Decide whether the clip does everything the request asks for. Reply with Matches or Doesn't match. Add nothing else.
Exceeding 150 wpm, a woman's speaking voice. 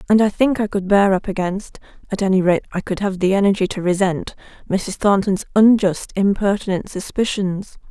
Matches